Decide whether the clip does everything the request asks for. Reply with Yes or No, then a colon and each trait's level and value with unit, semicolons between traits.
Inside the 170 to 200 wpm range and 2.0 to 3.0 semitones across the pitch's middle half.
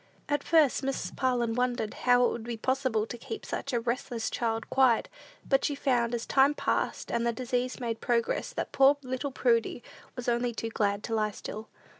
Yes: average, 195 wpm; narrow, 2.5 semitones